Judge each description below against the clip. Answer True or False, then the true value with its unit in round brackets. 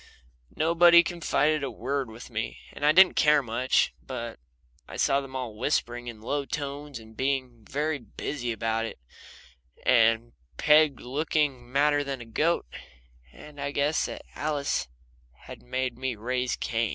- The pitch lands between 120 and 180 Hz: True (135 Hz)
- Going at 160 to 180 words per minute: False (150 wpm)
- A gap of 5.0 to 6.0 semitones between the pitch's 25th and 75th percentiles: False (3.9 semitones)